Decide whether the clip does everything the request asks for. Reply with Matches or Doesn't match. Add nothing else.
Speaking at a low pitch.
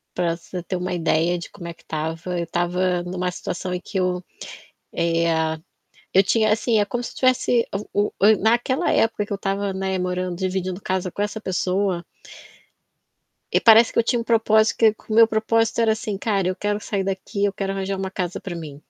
Doesn't match